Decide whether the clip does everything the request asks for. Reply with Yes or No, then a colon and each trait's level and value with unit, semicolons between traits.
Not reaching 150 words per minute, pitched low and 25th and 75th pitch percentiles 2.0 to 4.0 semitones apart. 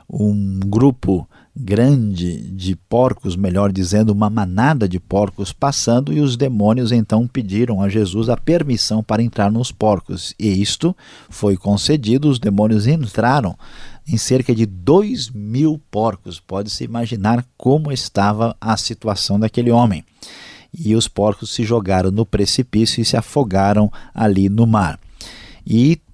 Yes: average, 140 wpm; low, 110 Hz; average, 3.4 semitones